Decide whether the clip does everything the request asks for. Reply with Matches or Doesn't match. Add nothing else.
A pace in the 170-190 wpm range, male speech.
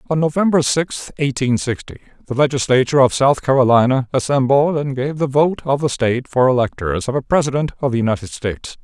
Matches